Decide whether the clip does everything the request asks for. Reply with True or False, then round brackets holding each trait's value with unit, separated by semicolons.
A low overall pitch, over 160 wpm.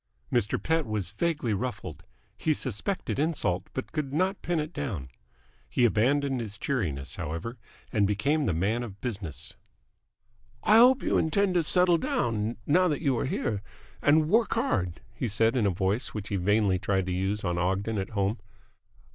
True (115 Hz; 170 wpm)